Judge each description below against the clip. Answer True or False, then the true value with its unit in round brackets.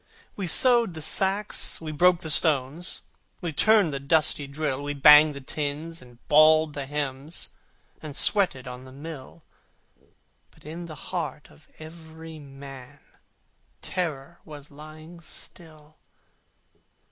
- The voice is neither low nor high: True (155 Hz)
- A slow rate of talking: True (130 wpm)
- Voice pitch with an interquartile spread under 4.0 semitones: True (2.7 semitones)